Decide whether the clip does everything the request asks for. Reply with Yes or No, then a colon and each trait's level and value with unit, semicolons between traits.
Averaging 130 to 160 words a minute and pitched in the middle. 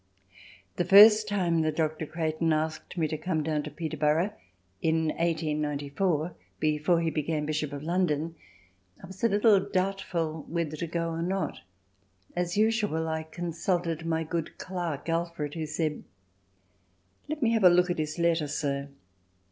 Yes: average, 155 wpm; medium, 165 Hz